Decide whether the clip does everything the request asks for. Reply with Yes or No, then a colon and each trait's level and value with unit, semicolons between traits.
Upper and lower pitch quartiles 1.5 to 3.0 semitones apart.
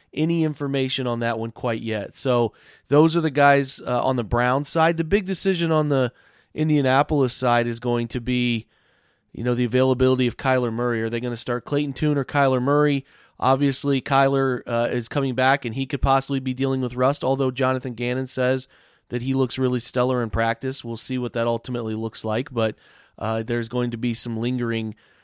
Yes: narrow, 2.5 semitones